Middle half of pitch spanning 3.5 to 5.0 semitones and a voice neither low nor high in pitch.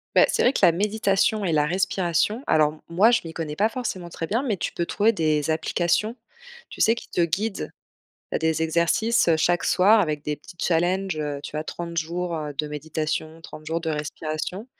Yes: average, 4.1 semitones; medium, 170 Hz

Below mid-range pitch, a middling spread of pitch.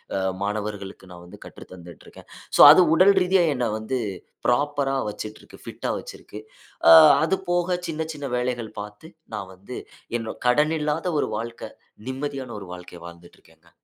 No: low, 125 Hz; wide, 6.6 semitones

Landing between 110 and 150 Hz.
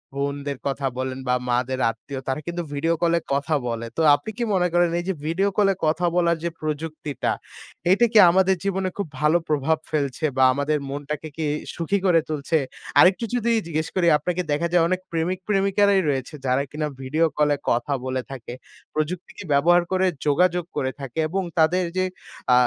No: medium, 160 Hz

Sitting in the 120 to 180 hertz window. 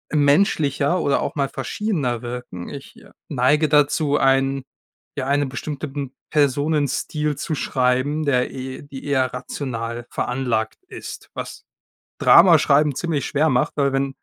Yes: medium, 140 Hz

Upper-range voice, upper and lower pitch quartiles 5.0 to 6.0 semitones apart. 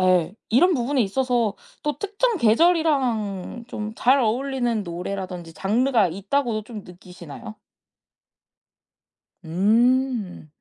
Yes: high, 225 Hz; wide, 5.4 semitones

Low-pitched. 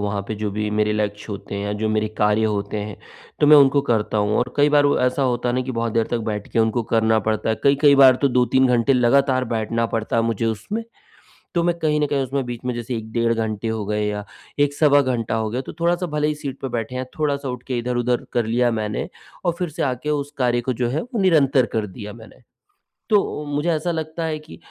Yes: low, 125 Hz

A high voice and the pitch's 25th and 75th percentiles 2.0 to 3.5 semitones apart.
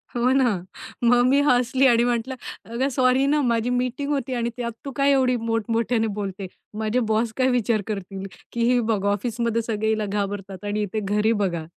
Yes: high, 230 Hz; average, 3.2 semitones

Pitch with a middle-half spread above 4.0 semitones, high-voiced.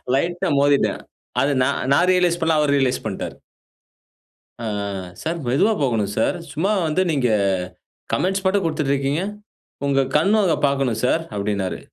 No: average, 4.5 semitones; medium, 145 Hz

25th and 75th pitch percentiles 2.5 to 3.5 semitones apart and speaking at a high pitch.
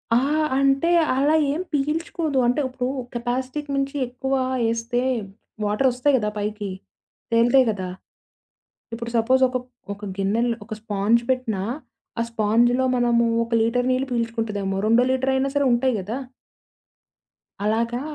Yes: average, 2.8 semitones; high, 245 Hz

